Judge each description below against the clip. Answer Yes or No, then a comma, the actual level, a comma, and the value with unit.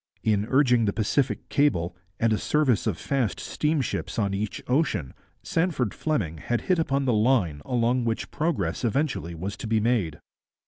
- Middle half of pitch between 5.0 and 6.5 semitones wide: Yes, wide, 5.5 semitones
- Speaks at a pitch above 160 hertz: No, low, 115 Hz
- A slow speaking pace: No, average, 165 wpm